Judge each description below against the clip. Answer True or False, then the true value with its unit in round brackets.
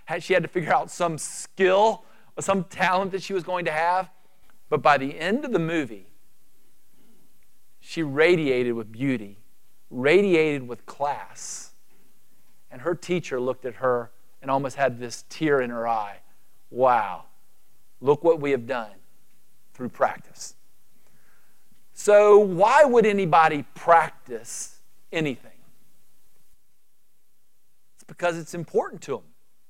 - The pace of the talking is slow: True (130 wpm)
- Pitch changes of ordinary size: False (5.9 semitones)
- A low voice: False (160 Hz)